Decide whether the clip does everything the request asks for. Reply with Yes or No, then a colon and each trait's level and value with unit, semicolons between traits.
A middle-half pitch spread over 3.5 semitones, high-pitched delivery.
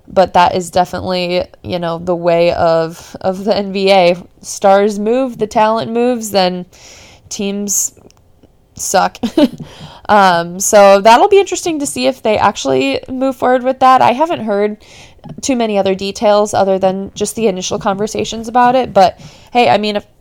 Yes: average, 4.2 semitones; high, 205 Hz